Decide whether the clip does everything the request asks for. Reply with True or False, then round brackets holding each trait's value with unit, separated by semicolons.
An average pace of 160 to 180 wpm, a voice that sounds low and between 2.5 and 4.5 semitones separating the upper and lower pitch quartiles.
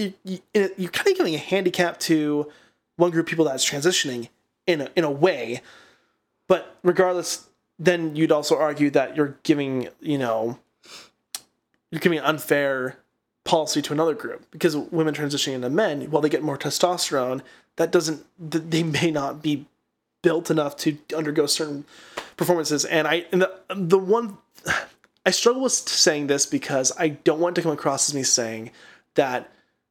False (165 wpm; 160 Hz; 3.4 semitones)